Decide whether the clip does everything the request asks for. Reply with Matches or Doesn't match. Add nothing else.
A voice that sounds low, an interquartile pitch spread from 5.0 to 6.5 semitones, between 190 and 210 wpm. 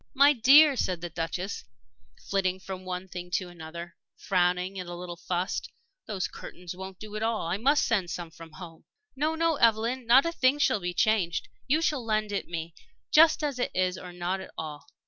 Doesn't match